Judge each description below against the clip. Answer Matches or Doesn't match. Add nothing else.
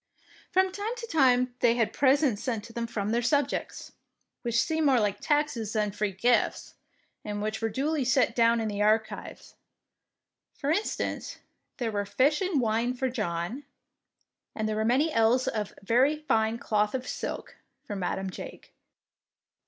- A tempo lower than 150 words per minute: Doesn't match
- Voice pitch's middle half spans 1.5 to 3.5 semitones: Doesn't match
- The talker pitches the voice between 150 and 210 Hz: Doesn't match